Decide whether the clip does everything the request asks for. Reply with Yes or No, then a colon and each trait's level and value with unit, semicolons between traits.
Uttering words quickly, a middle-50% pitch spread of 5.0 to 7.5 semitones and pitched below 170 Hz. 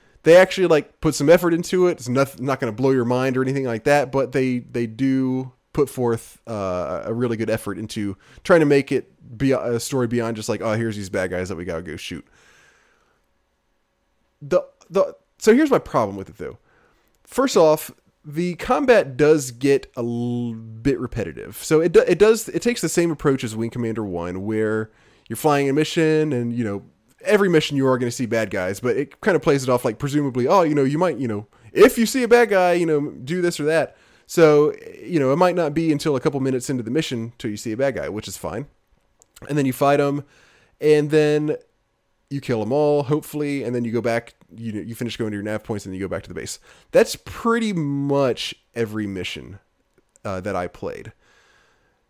Yes: fast, 225 wpm; wide, 5.4 semitones; low, 135 Hz